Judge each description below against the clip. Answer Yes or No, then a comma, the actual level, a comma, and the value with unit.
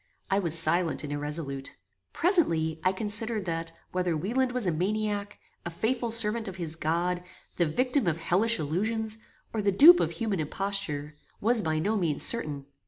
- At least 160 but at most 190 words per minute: Yes, average, 170 wpm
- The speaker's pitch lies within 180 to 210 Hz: Yes, high, 190 Hz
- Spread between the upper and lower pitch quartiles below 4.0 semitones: No, wide, 5.5 semitones